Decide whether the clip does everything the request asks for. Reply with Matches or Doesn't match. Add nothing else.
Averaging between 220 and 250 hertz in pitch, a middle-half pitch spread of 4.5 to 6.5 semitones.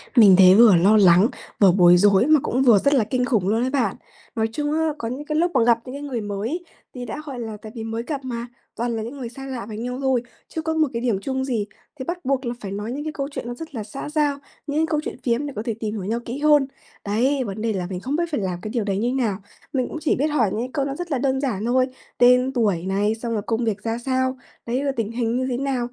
Doesn't match